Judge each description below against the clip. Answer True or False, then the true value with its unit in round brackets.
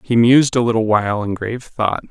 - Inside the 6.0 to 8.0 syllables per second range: True (6.3 syllables/s)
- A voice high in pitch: False (115 Hz)